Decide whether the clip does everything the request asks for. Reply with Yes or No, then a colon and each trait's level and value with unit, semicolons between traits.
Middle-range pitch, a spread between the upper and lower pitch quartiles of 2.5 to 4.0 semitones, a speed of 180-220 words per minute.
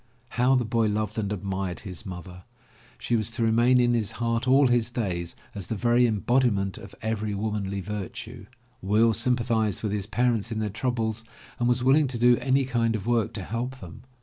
No: low, 115 Hz; average, 2.9 semitones; average, 195 wpm